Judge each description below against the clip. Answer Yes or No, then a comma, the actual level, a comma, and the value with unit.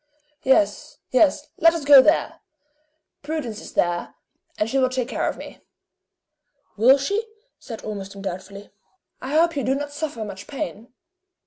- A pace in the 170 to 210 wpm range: No, average, 150 wpm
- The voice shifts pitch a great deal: Yes, wide, 5.7 semitones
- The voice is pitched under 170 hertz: No, very high, 260 Hz